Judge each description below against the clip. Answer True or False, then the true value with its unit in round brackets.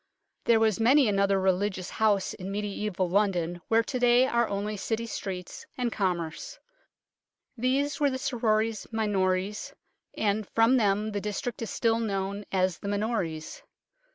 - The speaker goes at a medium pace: True (150 wpm)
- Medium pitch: False (210 Hz)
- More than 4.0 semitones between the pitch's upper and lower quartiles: False (2.9 semitones)